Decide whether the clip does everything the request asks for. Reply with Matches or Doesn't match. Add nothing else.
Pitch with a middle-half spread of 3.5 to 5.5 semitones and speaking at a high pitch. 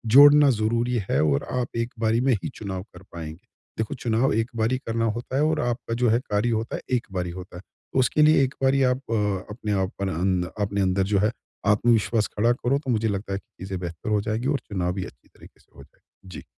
Doesn't match